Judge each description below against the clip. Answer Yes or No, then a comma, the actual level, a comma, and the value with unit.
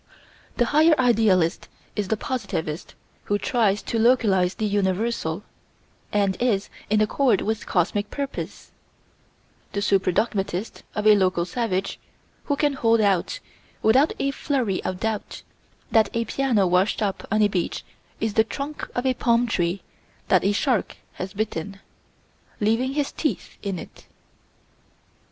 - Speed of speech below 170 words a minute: Yes, average, 140 wpm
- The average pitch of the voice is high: Yes, high, 215 Hz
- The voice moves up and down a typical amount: Yes, average, 3.9 semitones